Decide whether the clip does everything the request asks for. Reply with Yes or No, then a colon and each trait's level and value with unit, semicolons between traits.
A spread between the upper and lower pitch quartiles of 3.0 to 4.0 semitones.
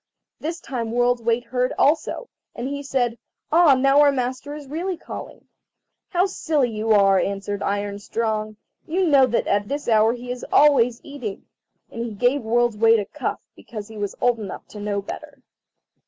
No: average, 4.6 semitones